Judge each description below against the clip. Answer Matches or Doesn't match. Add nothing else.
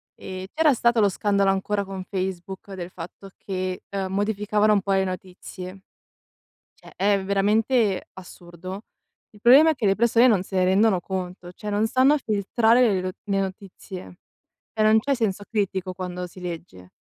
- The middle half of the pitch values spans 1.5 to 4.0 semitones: Matches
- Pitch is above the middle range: Matches